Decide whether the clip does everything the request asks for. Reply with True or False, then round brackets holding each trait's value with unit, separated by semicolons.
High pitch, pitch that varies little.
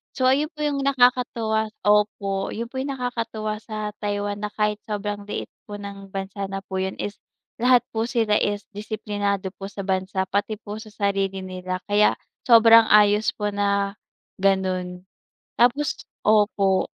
True (205 Hz; 2.0 semitones)